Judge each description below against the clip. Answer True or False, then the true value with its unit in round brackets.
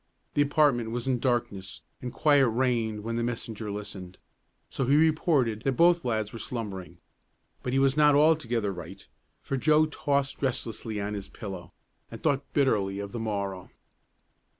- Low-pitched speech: True (120 Hz)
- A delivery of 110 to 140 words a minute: False (160 wpm)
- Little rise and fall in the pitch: False (5.2 semitones)